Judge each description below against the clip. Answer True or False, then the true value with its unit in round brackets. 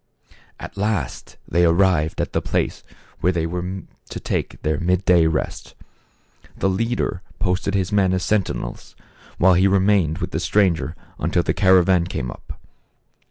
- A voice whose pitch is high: False (90 Hz)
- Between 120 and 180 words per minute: True (155 wpm)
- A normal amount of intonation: False (2.3 semitones)